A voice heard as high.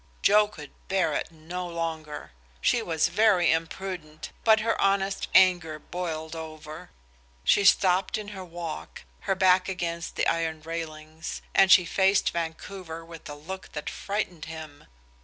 No: medium, 170 Hz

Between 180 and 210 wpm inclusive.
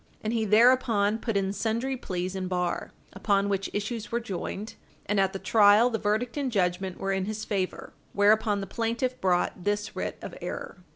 Yes: average, 185 wpm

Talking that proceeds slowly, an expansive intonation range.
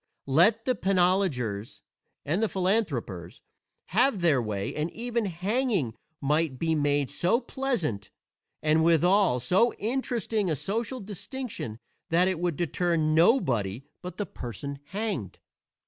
Yes: slow, 120 wpm; wide, 6.9 semitones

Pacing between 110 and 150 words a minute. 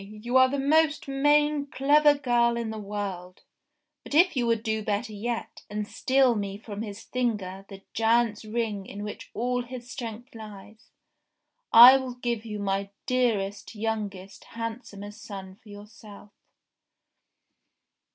Yes: average, 140 wpm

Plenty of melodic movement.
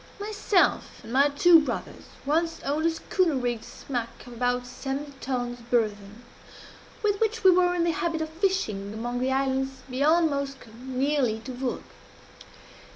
No: average, 5.0 semitones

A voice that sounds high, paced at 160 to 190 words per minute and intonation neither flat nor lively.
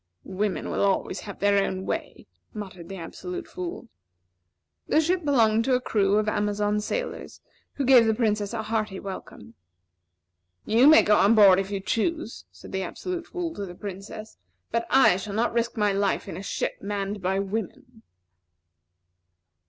Yes: high, 210 Hz; average, 170 wpm; average, 3.6 semitones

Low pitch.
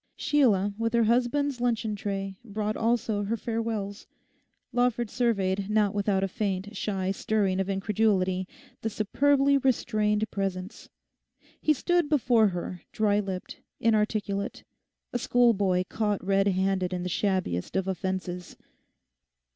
No: high, 205 Hz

